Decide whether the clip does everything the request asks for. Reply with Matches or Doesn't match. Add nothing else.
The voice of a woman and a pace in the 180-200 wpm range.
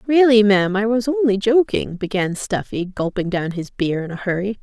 Matches